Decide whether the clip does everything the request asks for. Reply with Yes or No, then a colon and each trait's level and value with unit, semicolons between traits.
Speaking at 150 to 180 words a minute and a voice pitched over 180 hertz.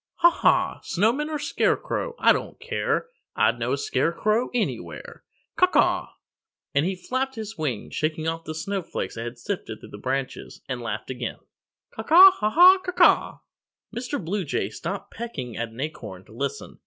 Yes: average, 175 wpm; high, 190 Hz